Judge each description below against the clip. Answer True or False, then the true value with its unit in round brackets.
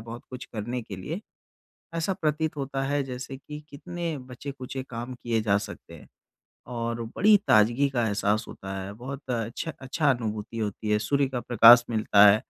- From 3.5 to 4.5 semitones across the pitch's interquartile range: True (4.1 semitones)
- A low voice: True (125 Hz)